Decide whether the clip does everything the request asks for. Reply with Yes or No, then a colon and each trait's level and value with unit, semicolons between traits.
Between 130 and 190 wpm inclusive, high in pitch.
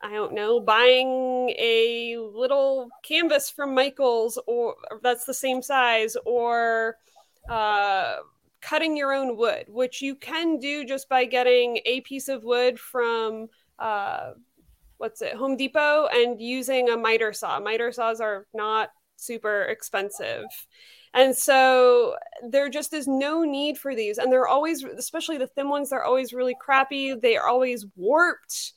Yes: average, 150 wpm; very high, 255 Hz